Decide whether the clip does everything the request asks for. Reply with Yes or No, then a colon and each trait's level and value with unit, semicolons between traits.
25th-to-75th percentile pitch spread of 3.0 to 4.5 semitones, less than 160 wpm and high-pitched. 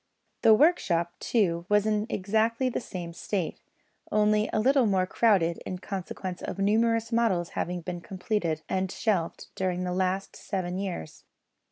Yes: average, 3.5 semitones; average, 150 wpm; high, 195 Hz